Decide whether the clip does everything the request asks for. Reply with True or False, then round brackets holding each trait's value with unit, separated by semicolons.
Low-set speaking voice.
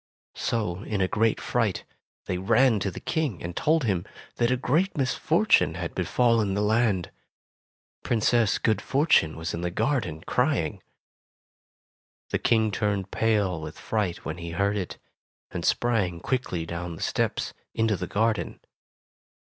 True (105 Hz)